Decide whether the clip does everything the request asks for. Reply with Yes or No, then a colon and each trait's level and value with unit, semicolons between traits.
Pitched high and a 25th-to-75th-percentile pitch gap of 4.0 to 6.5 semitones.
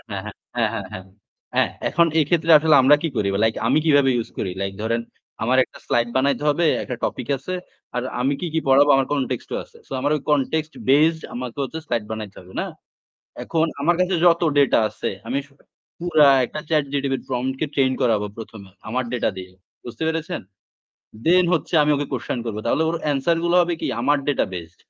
No: low, 135 Hz; average, 5.1 semitones